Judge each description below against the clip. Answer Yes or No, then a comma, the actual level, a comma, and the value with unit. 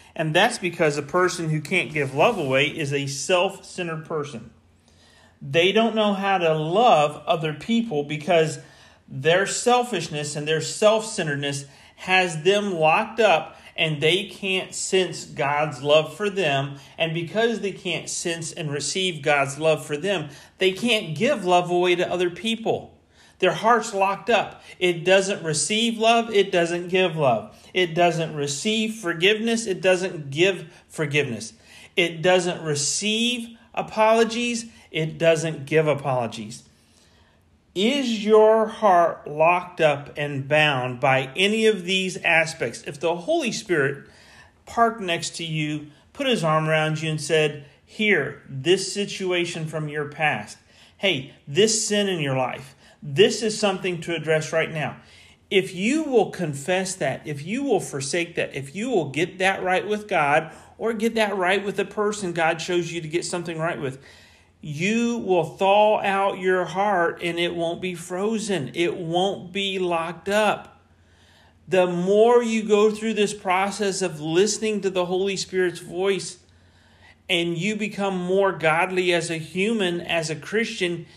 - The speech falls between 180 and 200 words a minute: No, average, 155 wpm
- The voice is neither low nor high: Yes, medium, 175 Hz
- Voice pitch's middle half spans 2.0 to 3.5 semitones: No, average, 4.2 semitones